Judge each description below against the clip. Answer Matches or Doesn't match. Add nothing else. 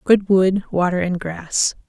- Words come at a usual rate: Matches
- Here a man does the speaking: Doesn't match